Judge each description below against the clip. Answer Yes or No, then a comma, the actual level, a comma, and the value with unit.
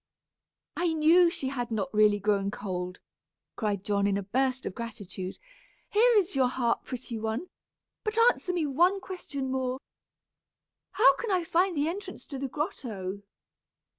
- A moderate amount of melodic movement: No, wide, 8.7 semitones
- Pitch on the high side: Yes, very high, 260 Hz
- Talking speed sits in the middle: Yes, average, 155 wpm